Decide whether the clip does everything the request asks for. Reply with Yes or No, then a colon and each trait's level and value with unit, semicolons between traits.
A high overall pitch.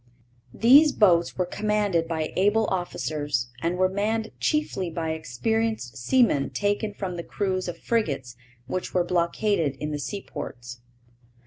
No: medium, 180 Hz